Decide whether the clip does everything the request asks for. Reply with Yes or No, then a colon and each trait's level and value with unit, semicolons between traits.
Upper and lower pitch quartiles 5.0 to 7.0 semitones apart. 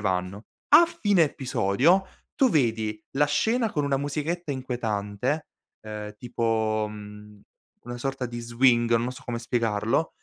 Yes: average, 5.3 semitones